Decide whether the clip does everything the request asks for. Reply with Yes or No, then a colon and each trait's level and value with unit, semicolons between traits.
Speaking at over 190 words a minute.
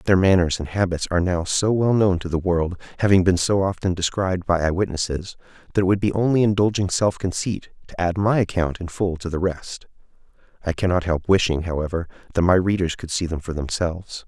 Yes: fast, 205 wpm